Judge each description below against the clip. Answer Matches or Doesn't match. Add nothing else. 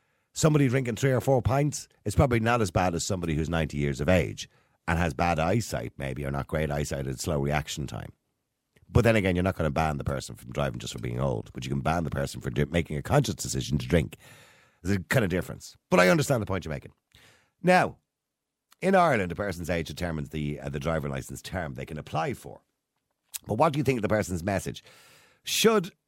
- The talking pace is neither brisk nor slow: Doesn't match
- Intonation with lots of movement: Matches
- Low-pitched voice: Matches